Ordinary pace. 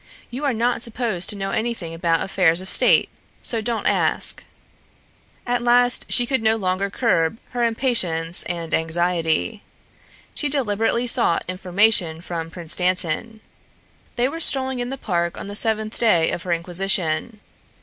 Yes: average, 150 wpm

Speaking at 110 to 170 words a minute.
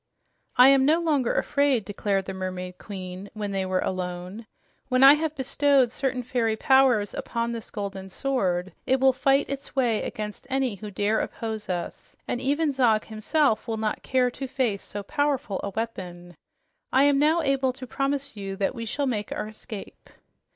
No: average, 180 wpm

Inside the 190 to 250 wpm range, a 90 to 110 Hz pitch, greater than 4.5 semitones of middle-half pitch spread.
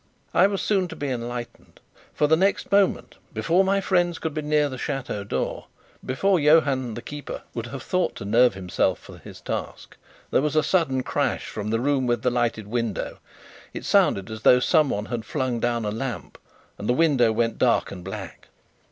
No: average, 195 wpm; low, 130 Hz; average, 5.1 semitones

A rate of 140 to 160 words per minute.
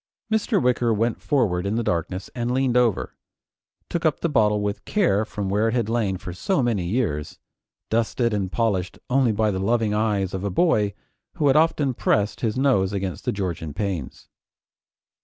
No: average, 180 wpm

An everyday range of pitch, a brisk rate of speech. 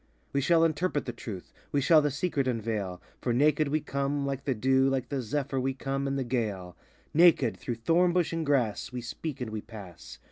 Yes: average, 3.9 semitones; fast, 210 wpm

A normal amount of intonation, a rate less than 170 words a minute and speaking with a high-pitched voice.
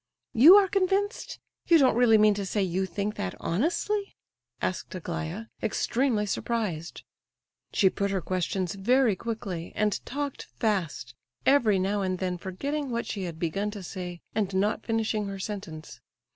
Yes: average, 4.2 semitones; average, 155 wpm; high, 205 Hz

